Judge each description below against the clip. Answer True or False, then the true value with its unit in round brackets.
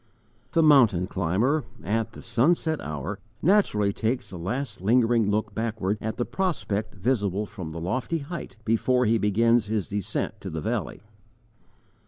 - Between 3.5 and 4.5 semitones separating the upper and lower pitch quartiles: True (4.0 semitones)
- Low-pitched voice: True (110 Hz)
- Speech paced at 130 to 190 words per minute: True (150 wpm)